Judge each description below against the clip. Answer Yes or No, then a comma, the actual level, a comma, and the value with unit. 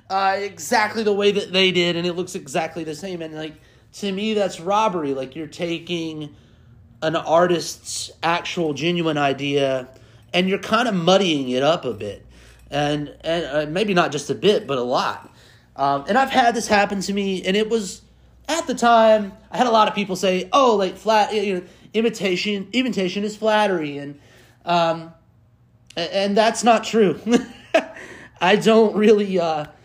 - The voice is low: No, medium, 180 Hz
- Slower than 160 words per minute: No, average, 175 wpm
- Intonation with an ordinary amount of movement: No, wide, 5.7 semitones